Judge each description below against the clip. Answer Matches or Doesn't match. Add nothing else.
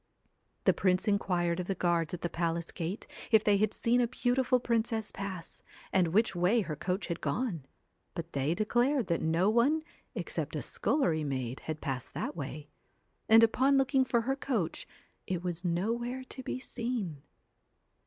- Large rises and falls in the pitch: Matches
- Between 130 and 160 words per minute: Doesn't match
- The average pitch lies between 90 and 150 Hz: Doesn't match